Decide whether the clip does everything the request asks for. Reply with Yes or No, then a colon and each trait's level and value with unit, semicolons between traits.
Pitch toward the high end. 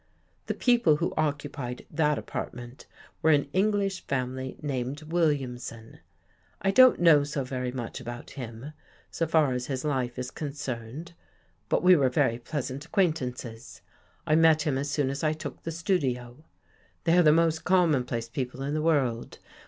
No: medium, 145 Hz